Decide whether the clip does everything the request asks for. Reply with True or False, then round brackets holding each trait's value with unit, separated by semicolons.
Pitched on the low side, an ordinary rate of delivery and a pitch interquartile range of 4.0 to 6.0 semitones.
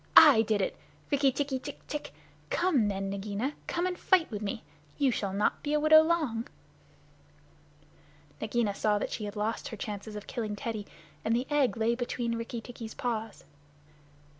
False (230 Hz; 170 wpm; 5.1 semitones)